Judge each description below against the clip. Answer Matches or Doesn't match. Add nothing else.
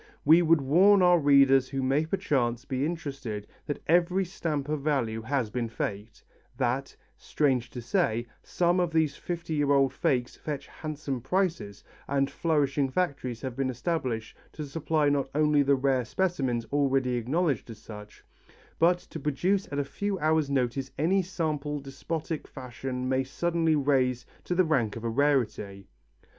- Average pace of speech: Matches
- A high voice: Doesn't match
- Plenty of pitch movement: Doesn't match